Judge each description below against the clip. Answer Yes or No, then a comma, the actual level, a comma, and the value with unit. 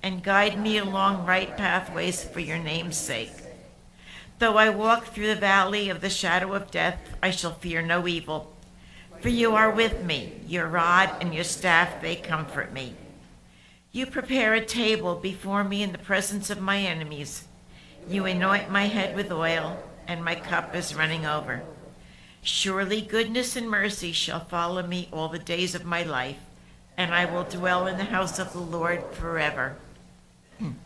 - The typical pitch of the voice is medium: Yes, medium, 180 Hz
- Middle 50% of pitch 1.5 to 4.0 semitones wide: Yes, average, 3.3 semitones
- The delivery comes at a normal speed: Yes, average, 170 wpm